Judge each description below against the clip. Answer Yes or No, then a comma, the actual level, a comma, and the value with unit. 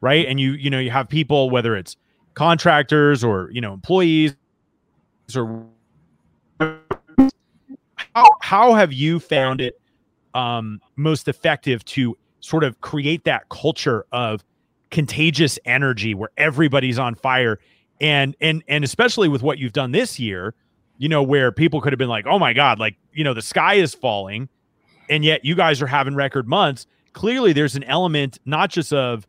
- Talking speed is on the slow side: No, average, 165 wpm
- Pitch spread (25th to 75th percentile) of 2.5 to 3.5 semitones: No, average, 4.3 semitones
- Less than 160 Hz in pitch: Yes, medium, 140 Hz